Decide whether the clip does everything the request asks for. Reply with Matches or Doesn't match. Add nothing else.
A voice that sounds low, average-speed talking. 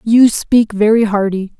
Doesn't match